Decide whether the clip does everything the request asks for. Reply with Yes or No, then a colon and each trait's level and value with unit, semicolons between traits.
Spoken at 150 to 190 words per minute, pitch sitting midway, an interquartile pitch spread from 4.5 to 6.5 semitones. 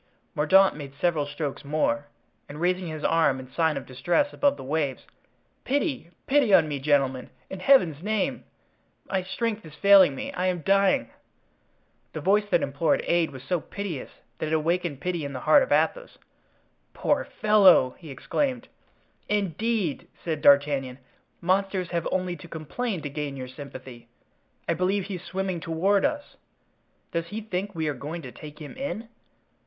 Yes: average, 165 wpm; medium, 170 Hz; average, 5.2 semitones